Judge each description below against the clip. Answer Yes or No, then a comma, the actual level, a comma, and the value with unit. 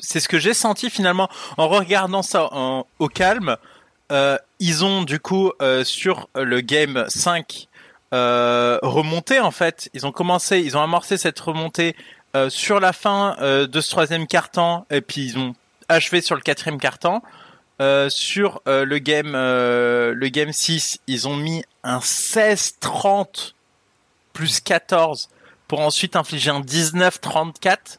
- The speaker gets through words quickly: No, average, 155 wpm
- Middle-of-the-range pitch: Yes, medium, 160 Hz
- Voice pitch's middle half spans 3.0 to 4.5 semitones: No, average, 4.9 semitones